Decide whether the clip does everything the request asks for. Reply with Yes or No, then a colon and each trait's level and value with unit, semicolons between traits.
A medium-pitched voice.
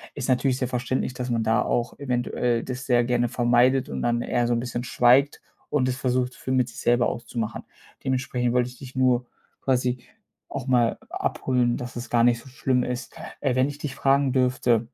No: low, 125 Hz